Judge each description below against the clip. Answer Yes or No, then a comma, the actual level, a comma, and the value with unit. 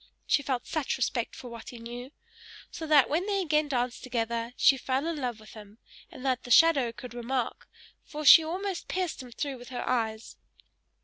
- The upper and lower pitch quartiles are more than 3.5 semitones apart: Yes, average, 4.2 semitones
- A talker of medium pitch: No, very high, 255 Hz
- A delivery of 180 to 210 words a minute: Yes, average, 195 wpm